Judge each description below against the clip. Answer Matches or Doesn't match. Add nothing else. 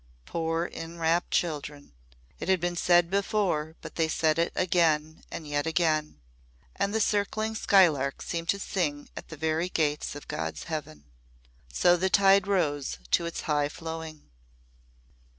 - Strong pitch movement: Doesn't match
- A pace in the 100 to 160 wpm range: Matches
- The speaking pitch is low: Doesn't match